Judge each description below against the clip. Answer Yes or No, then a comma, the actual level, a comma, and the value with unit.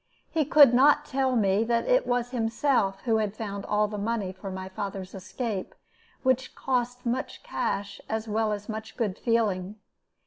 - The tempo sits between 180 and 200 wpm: No, average, 170 wpm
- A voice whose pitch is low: No, high, 220 Hz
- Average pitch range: Yes, average, 3.6 semitones